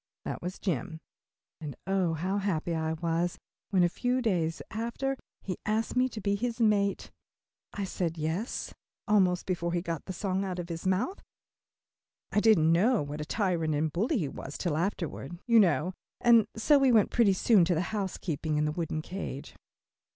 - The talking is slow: No, average, 180 wpm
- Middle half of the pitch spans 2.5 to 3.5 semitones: No, average, 4.4 semitones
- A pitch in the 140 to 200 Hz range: Yes, medium, 185 Hz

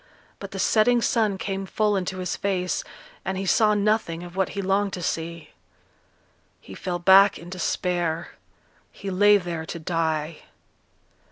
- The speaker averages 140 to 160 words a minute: Yes, average, 155 wpm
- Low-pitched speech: No, medium, 185 Hz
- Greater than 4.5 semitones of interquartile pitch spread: No, average, 2.8 semitones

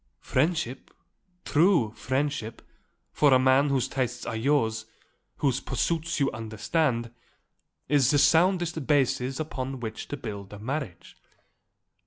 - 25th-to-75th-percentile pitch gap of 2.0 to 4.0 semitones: No, average, 4.5 semitones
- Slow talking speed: Yes, slow, 120 wpm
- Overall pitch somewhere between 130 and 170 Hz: Yes, low, 135 Hz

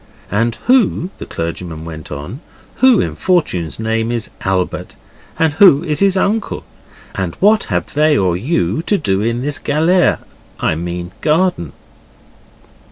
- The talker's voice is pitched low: Yes, low, 120 Hz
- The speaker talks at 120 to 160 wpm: Yes, average, 145 wpm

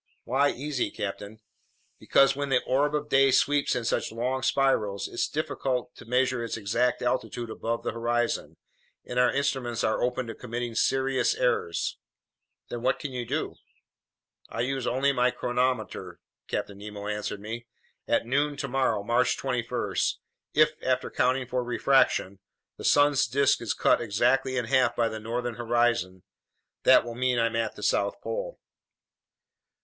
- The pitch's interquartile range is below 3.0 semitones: Yes, narrow, 2.6 semitones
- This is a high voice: No, low, 125 Hz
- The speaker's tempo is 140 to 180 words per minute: Yes, average, 155 wpm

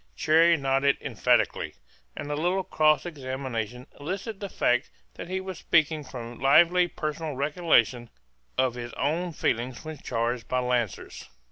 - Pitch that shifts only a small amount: No, average, 5.0 semitones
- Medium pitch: Yes, medium, 145 Hz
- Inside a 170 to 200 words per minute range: No, average, 140 wpm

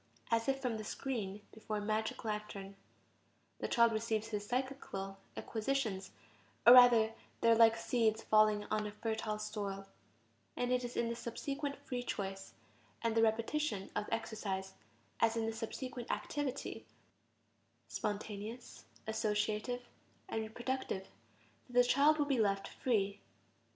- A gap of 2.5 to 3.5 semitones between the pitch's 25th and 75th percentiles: Yes, average, 2.8 semitones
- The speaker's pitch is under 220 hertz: No, high, 225 Hz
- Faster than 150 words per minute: No, average, 140 wpm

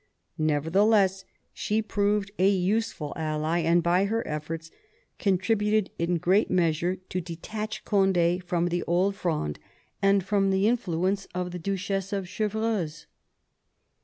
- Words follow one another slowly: Yes, slow, 130 wpm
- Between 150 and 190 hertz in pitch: Yes, medium, 185 Hz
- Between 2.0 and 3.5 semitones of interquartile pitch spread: Yes, average, 2.9 semitones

